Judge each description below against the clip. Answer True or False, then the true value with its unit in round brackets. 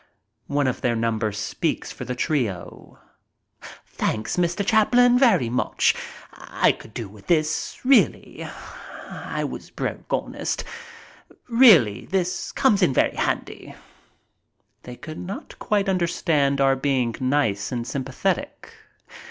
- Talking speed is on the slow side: True (120 wpm)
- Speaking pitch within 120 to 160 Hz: True (140 Hz)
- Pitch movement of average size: False (8.0 semitones)